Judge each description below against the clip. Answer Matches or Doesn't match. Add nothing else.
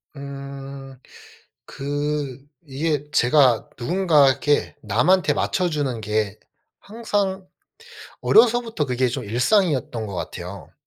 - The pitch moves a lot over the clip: Doesn't match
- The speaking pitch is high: Doesn't match